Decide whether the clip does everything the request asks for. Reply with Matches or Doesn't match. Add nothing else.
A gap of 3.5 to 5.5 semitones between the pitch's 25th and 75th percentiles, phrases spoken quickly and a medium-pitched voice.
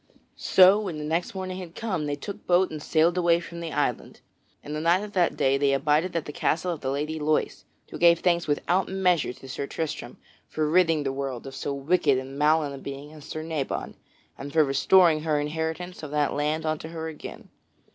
Doesn't match